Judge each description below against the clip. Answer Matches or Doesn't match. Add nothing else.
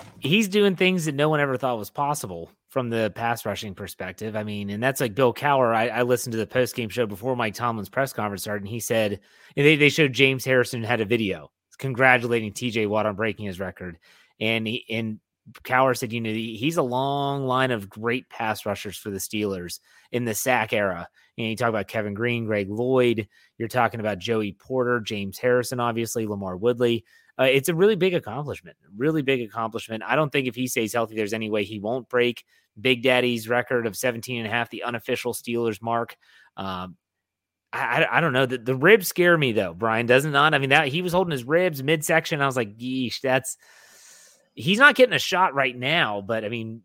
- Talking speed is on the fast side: Matches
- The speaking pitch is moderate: Doesn't match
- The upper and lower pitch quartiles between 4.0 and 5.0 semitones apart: Doesn't match